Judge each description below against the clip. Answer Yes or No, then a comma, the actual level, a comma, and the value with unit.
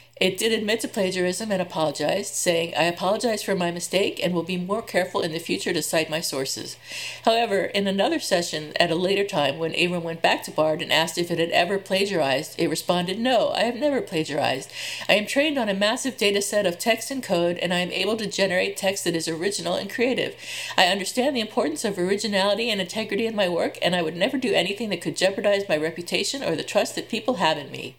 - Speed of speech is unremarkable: No, fast, 230 wpm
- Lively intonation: No, average, 4.3 semitones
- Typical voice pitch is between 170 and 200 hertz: Yes, high, 190 Hz